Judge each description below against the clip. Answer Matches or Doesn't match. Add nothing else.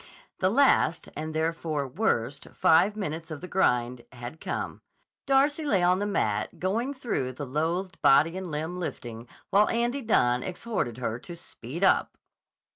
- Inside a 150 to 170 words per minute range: Matches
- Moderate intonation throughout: Doesn't match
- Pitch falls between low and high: Matches